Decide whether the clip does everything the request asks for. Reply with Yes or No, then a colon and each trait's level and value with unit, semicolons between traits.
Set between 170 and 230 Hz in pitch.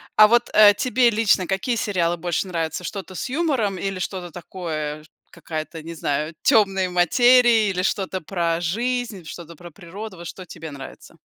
Yes: medium, 185 Hz